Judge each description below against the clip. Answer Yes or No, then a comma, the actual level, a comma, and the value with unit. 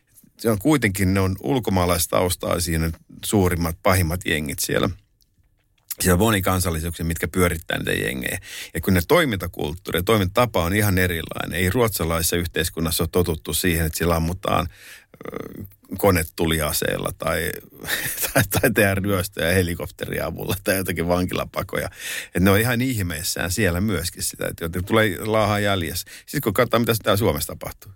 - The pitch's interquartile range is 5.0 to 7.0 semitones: No, average, 3.3 semitones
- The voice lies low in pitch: Yes, very low, 95 Hz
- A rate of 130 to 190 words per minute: Yes, average, 150 wpm